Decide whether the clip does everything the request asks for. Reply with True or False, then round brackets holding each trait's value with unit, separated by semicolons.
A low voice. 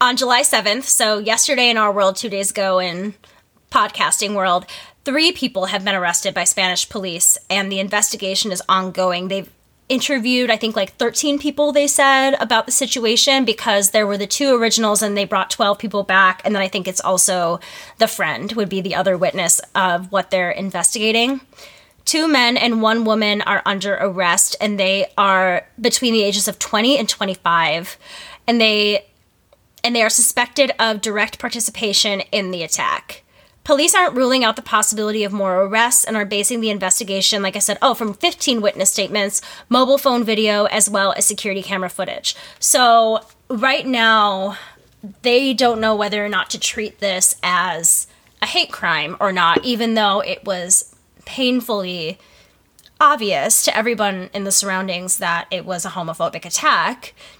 False (210 Hz)